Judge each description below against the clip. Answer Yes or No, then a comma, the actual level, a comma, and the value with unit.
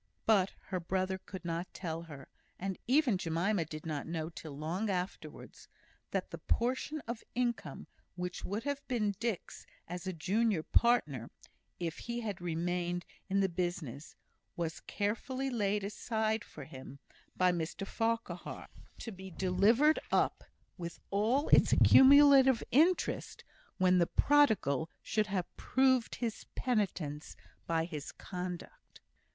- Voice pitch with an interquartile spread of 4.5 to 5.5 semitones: Yes, average, 5.2 semitones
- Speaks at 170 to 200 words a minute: No, slow, 135 wpm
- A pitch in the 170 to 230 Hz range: Yes, high, 190 Hz